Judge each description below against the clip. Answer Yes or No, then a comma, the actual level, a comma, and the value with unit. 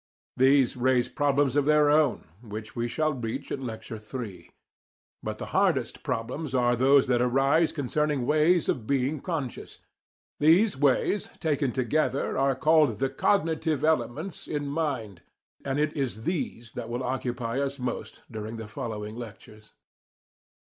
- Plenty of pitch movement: No, average, 4.0 semitones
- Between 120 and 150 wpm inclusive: Yes, average, 145 wpm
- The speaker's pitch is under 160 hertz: Yes, low, 135 Hz